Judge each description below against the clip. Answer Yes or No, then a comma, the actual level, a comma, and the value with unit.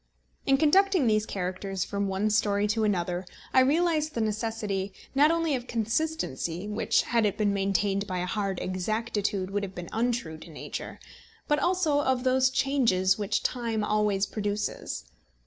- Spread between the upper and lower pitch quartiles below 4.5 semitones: No, average, 4.9 semitones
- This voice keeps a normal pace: Yes, average, 160 wpm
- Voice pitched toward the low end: No, high, 210 Hz